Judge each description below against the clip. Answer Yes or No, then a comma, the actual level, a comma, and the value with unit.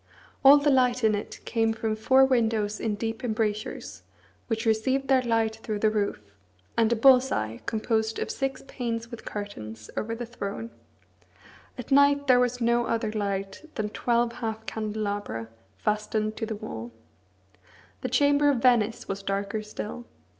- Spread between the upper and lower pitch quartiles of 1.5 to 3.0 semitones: Yes, narrow, 2.6 semitones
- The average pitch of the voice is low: No, high, 225 Hz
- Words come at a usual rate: Yes, average, 160 wpm